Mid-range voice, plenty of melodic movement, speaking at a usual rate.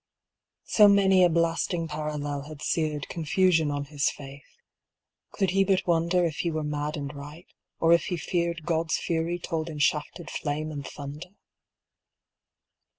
No: medium, 160 Hz; narrow, 2.6 semitones; average, 155 wpm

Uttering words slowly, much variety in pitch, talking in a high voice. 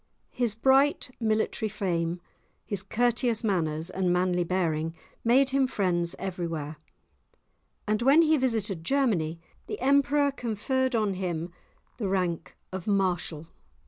Yes: slow, 120 wpm; wide, 6.1 semitones; high, 200 Hz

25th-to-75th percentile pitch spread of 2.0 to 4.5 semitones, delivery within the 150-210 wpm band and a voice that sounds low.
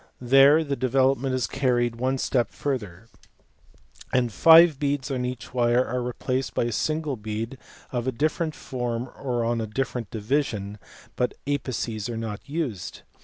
Yes: average, 2.9 semitones; average, 155 wpm; low, 125 Hz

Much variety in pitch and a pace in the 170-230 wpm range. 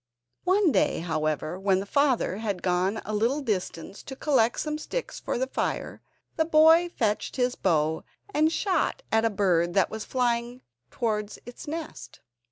Yes: wide, 7.3 semitones; average, 175 wpm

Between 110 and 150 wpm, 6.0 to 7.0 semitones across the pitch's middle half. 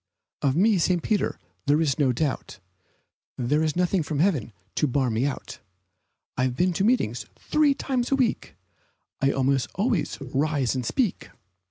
No: average, 170 wpm; wide, 6.7 semitones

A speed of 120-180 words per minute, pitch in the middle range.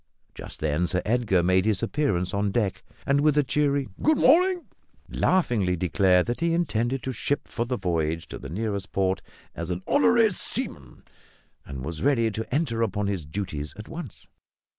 No: average, 175 wpm; low, 110 Hz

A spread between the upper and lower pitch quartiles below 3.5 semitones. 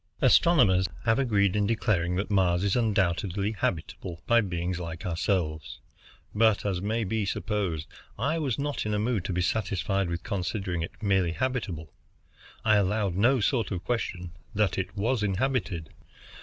No: average, 3.9 semitones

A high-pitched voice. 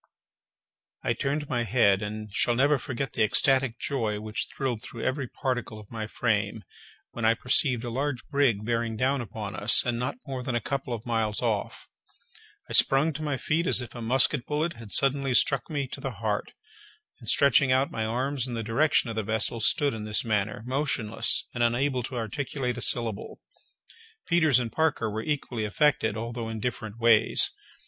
No: low, 120 Hz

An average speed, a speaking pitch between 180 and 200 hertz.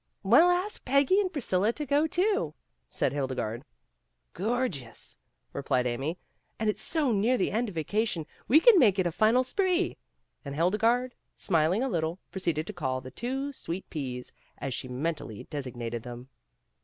Yes: average, 160 wpm; high, 190 Hz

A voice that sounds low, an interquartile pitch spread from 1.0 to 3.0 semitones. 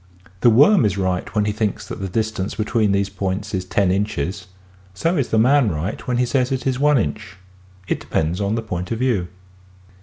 No: low, 105 Hz; average, 4.5 semitones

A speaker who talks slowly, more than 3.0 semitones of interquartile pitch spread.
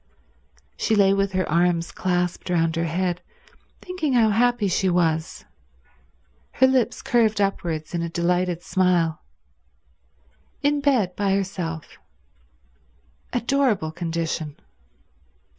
Yes: slow, 110 wpm; average, 4.4 semitones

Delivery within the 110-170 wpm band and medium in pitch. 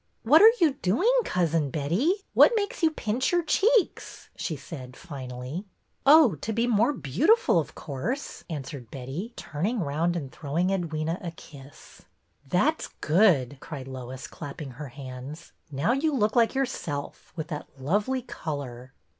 Yes: average, 165 wpm; medium, 165 Hz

